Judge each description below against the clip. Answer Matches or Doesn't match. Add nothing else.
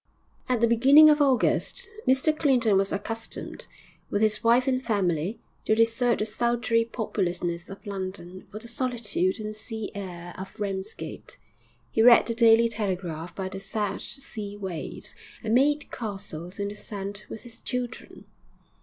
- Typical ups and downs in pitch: Matches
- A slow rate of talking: Doesn't match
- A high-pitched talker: Matches